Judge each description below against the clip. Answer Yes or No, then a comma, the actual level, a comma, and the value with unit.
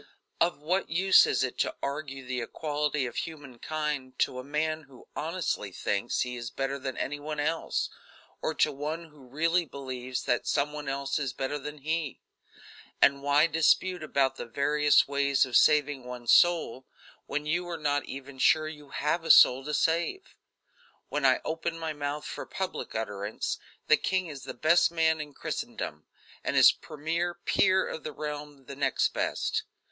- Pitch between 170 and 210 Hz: No, medium, 145 Hz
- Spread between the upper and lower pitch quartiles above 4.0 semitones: No, average, 2.9 semitones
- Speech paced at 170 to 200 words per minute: Yes, average, 175 wpm